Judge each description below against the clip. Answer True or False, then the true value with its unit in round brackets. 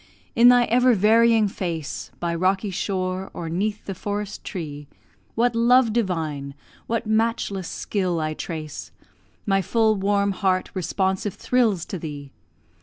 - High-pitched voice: True (195 Hz)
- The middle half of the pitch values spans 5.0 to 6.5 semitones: False (4.3 semitones)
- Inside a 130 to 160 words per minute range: True (135 wpm)